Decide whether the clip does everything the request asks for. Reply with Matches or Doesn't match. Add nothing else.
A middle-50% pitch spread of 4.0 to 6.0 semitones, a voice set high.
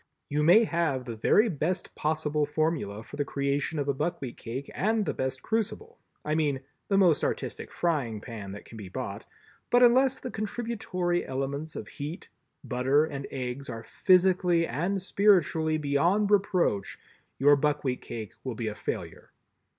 Doesn't match